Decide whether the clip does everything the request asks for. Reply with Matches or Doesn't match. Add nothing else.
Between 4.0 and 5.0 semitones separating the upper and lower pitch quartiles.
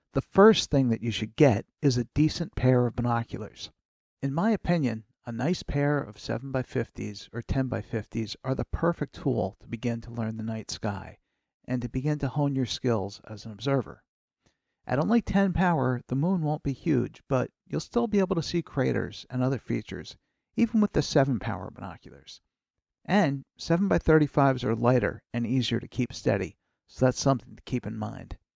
Matches